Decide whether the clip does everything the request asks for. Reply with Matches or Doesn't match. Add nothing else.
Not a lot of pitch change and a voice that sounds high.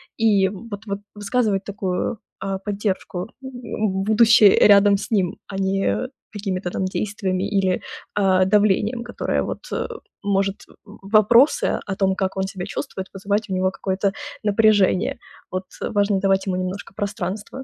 Matches